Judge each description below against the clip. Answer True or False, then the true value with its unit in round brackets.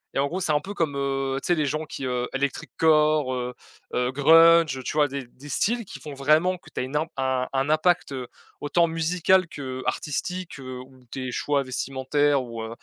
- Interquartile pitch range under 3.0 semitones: False (3.4 semitones)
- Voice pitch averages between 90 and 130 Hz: False (140 Hz)